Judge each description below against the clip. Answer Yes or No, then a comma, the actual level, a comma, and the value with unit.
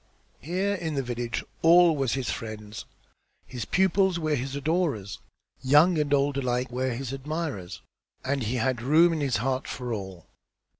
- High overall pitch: No, low, 135 Hz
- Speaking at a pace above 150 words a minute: Yes, average, 165 wpm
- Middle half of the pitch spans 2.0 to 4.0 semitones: No, average, 4.6 semitones